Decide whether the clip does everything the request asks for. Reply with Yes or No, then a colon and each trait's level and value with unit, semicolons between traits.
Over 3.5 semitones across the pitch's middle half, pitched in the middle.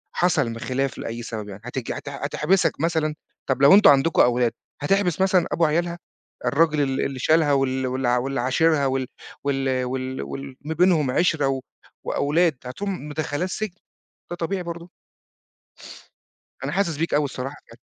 Yes: average, 4.2 semitones; medium, 145 Hz